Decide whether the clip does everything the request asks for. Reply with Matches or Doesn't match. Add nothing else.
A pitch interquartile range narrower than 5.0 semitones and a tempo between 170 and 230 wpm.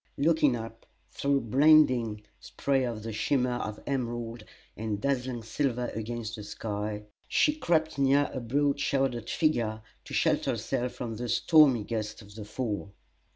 Doesn't match